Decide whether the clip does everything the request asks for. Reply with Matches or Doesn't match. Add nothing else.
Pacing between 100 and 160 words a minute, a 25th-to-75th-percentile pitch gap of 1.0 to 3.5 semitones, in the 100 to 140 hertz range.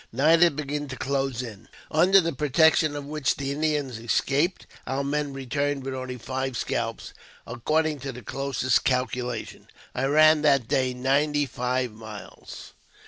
Matches